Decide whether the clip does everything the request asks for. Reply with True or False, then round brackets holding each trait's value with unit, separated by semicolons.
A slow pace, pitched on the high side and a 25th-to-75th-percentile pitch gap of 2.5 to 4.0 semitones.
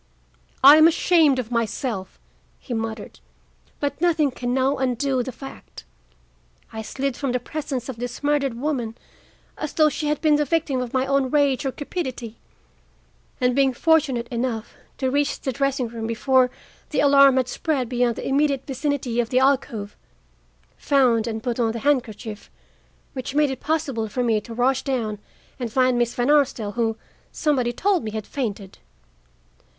False (165 wpm; 260 Hz; 3.2 semitones)